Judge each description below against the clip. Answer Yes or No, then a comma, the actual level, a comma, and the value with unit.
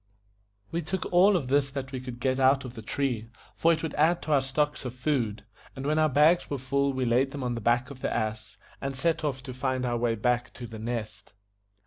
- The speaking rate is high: Yes, fast, 245 wpm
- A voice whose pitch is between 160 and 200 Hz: No, low, 130 Hz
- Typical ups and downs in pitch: Yes, average, 3.2 semitones